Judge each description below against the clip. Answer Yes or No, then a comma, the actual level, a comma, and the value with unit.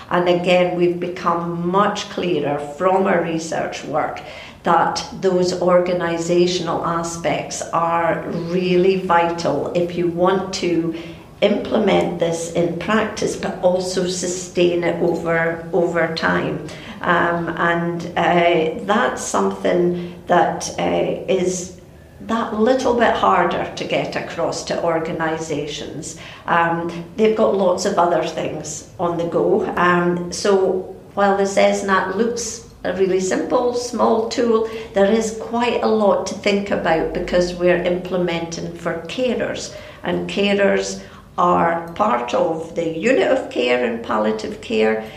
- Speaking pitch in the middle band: Yes, medium, 175 Hz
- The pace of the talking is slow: Yes, slow, 125 wpm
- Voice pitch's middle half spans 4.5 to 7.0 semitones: No, narrow, 2.3 semitones